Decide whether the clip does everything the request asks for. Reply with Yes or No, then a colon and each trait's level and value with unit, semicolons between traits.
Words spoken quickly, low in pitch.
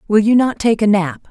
No: fast, 275 wpm; high, 210 Hz